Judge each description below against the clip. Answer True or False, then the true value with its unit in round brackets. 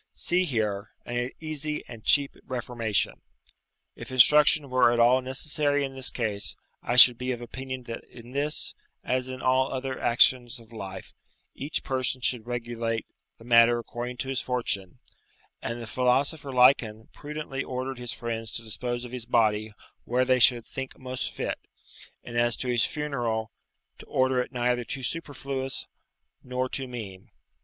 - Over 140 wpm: True (160 wpm)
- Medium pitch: False (125 Hz)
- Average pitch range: False (2.1 semitones)